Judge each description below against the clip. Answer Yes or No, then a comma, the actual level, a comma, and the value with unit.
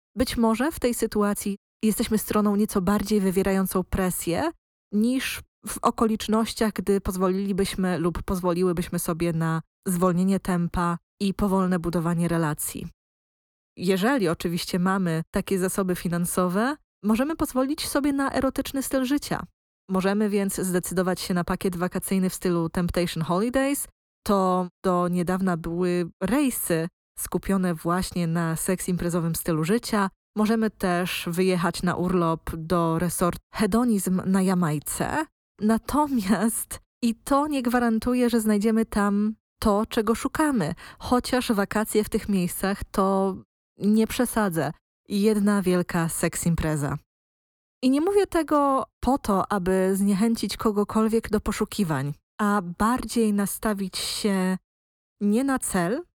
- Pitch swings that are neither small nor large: Yes, average, 3.9 semitones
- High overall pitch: Yes, high, 195 Hz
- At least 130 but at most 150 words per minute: No, average, 120 wpm